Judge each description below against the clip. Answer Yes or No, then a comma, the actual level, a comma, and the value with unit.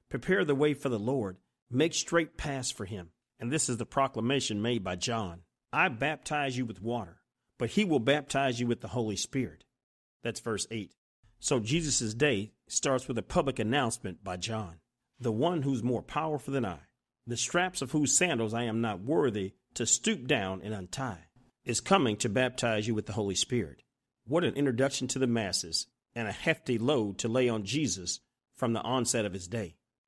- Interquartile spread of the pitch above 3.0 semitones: Yes, average, 4.0 semitones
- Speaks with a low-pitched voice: Yes, low, 120 Hz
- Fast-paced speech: No, average, 190 wpm